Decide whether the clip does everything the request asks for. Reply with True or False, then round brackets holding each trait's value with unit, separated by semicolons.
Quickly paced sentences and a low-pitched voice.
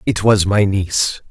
False (185 wpm; 100 Hz)